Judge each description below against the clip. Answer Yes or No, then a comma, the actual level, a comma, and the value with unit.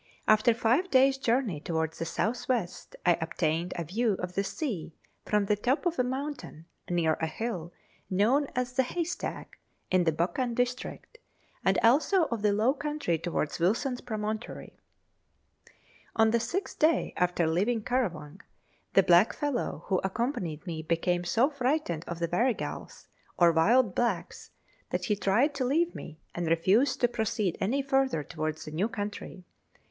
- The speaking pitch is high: Yes, high, 215 Hz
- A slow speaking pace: No, average, 155 wpm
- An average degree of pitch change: No, wide, 6.7 semitones